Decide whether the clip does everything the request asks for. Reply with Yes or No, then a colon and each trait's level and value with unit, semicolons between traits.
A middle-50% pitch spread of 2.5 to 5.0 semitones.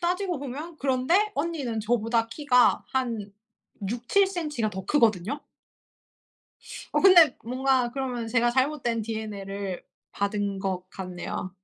No: wide, 5.5 semitones